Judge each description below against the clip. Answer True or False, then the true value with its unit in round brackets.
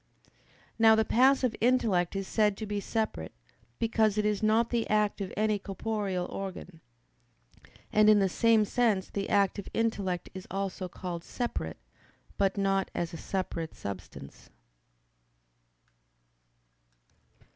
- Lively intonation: False (2.7 semitones)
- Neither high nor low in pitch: False (205 Hz)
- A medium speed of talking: False (125 wpm)